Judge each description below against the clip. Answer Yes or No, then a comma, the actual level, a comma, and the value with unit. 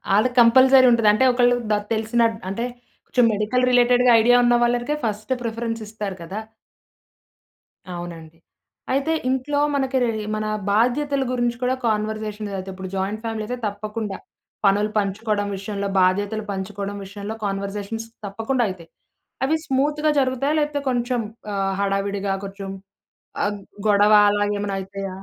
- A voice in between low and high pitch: No, high, 215 Hz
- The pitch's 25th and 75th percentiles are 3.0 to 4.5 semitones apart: Yes, average, 3.6 semitones